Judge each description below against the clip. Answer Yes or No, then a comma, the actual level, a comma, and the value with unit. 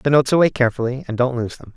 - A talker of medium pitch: No, low, 125 Hz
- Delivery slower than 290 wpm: No, fast, 305 wpm